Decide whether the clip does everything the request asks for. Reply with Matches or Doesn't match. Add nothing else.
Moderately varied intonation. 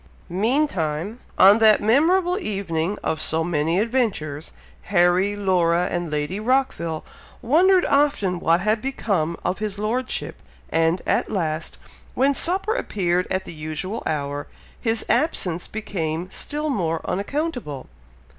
Doesn't match